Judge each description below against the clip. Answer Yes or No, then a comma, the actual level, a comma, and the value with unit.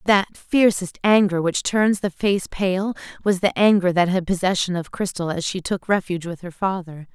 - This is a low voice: No, medium, 185 Hz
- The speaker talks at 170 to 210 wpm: Yes, average, 195 wpm